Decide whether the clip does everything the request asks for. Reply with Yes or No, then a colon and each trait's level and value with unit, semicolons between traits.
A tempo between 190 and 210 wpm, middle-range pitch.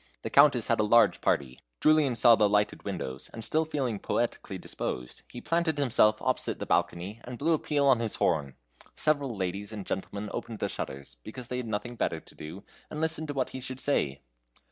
No: fast, 205 wpm; low, 115 Hz